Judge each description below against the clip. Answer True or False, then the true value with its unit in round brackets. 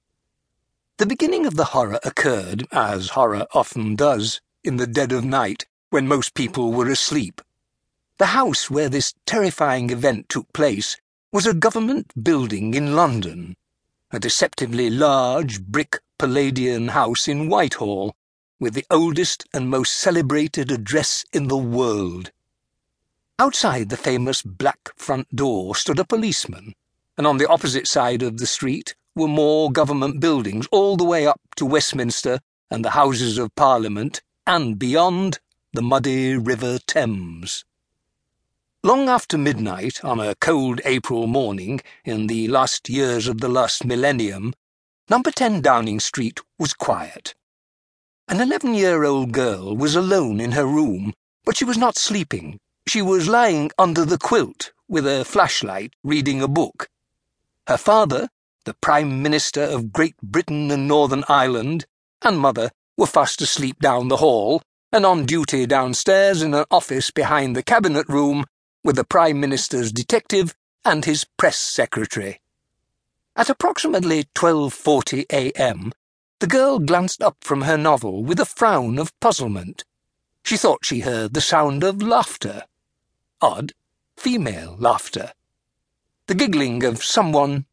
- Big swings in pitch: False (4.9 semitones)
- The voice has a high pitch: False (140 Hz)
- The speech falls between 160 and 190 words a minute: False (145 wpm)